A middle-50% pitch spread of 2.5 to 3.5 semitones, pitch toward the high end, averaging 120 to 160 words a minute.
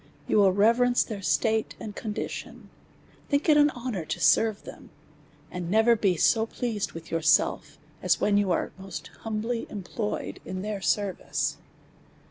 Yes: average, 3.0 semitones; high, 210 Hz; average, 145 wpm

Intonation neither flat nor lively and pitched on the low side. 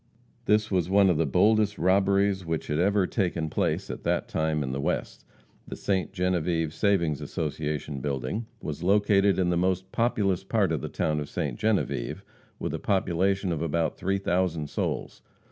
Yes: average, 3.7 semitones; very low, 90 Hz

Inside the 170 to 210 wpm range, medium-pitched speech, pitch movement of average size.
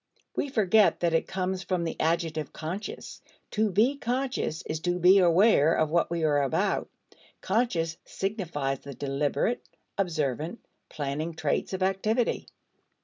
No: average, 140 wpm; medium, 175 Hz; average, 4.3 semitones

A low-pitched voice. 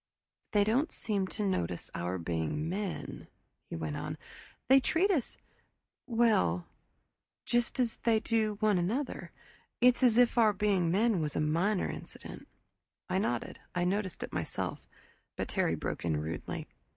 No: high, 205 Hz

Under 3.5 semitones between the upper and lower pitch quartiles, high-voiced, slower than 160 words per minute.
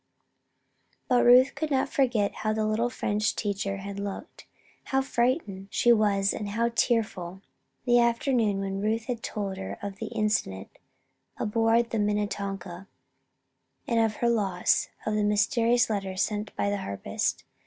Yes: average, 2.9 semitones; high, 215 Hz; average, 150 wpm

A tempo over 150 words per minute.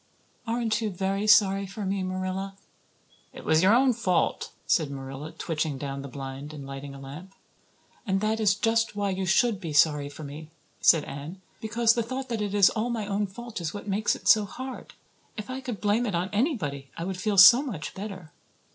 Yes: fast, 205 wpm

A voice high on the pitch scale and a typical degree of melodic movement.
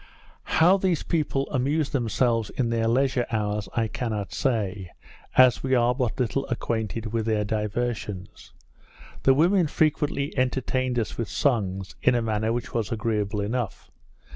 No: low, 120 Hz; average, 3.5 semitones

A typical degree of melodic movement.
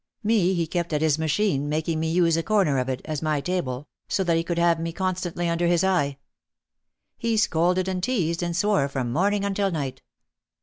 Yes: average, 3.2 semitones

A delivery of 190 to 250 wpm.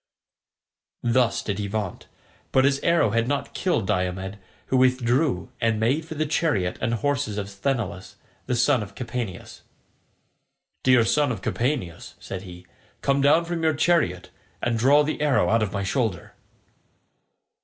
No: average, 155 wpm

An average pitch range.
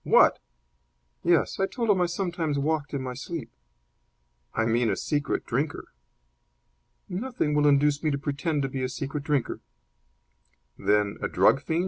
Yes: average, 3.5 semitones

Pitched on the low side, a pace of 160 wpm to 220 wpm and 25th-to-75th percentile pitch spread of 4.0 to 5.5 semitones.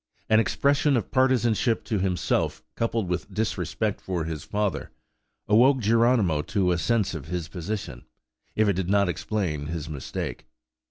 No: low, 100 Hz; average, 150 wpm; average, 4.9 semitones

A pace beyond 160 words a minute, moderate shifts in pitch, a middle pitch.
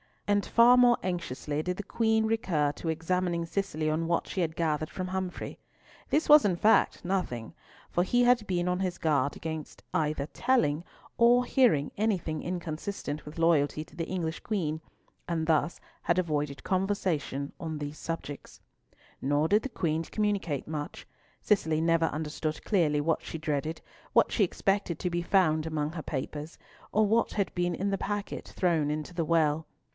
Yes: average, 170 wpm; average, 4.0 semitones; medium, 170 Hz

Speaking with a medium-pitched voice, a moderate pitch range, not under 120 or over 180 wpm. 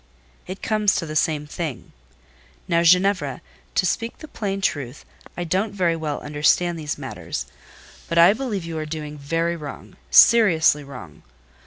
Yes: medium, 165 Hz; average, 4.4 semitones; average, 150 wpm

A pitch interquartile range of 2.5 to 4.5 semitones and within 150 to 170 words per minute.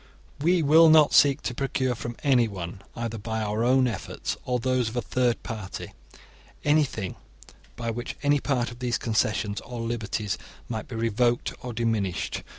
Yes: average, 2.8 semitones; average, 165 wpm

